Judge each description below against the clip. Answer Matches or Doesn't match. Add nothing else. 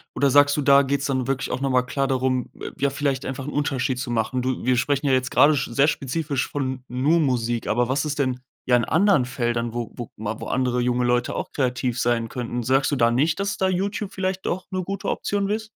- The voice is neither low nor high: Doesn't match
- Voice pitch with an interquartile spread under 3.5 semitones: Matches